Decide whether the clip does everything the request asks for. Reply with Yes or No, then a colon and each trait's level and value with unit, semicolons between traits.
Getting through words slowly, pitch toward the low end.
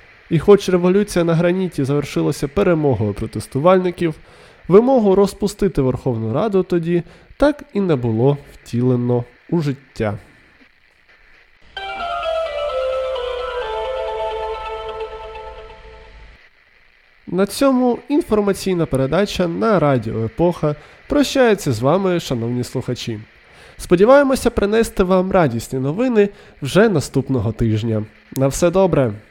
No: slow, 90 wpm; medium, 180 Hz